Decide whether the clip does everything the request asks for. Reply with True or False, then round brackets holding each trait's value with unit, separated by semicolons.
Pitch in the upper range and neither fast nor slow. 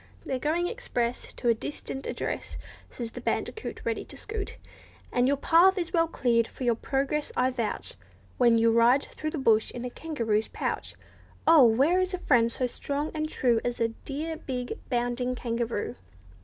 True (255 Hz; 180 wpm)